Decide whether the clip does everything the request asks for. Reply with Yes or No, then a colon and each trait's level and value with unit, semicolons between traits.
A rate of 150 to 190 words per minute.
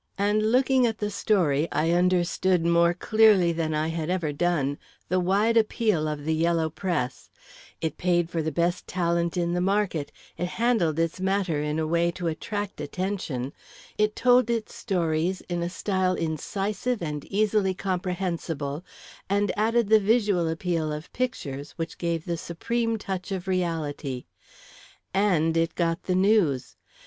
Yes: average, 155 wpm